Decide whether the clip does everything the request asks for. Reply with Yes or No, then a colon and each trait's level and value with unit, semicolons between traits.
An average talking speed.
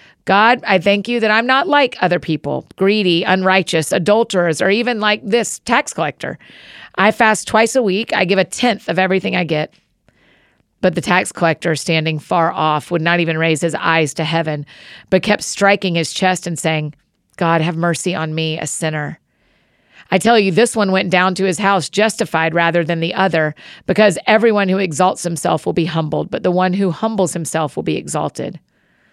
Yes: average, 190 wpm